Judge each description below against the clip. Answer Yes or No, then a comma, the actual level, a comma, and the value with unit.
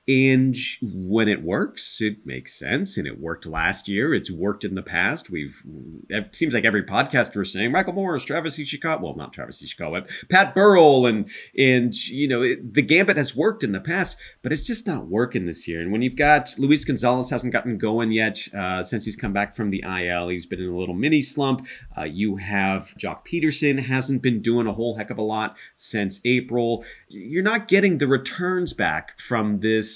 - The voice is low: Yes, low, 120 Hz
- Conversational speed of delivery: No, fast, 210 wpm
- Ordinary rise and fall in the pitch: No, wide, 5.7 semitones